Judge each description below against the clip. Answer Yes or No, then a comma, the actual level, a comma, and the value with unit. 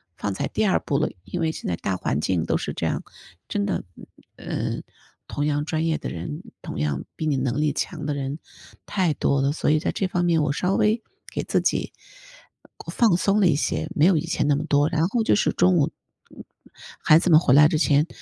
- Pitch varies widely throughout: No, average, 4.0 semitones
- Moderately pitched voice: Yes, medium, 150 Hz